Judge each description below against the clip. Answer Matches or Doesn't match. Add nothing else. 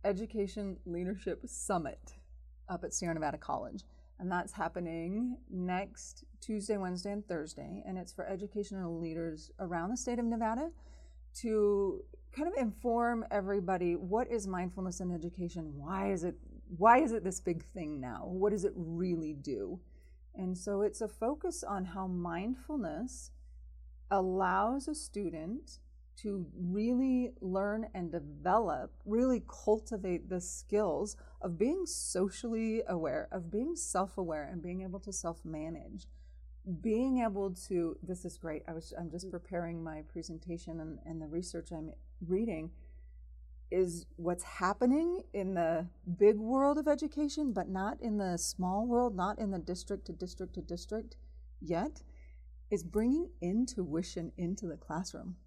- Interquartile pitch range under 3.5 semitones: Doesn't match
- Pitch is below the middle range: Doesn't match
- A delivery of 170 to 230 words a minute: Doesn't match